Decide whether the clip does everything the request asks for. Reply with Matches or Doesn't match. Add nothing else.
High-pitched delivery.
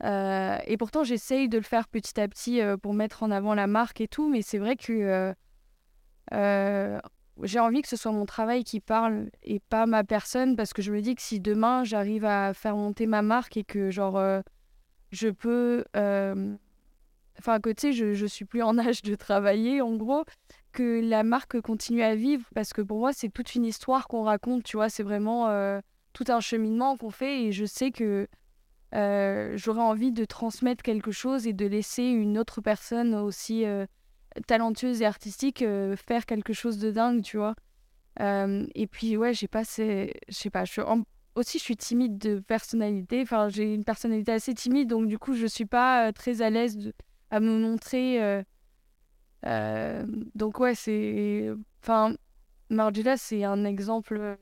Matches